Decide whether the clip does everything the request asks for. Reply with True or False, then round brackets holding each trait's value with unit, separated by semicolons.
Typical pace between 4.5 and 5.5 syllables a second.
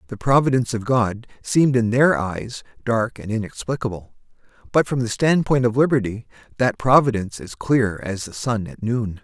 True (5.1 syllables/s)